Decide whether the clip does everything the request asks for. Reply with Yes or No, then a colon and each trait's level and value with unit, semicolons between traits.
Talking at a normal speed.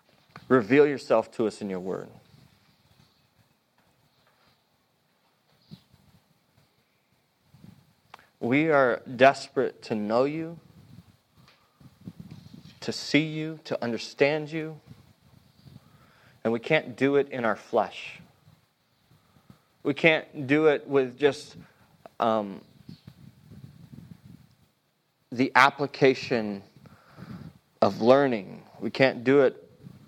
No: slow, 85 wpm